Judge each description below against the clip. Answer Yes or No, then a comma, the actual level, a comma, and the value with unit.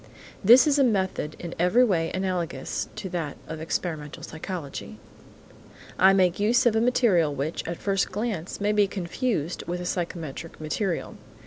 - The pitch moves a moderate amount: Yes, average, 4.1 semitones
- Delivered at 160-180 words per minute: No, average, 150 wpm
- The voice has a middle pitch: Yes, medium, 180 Hz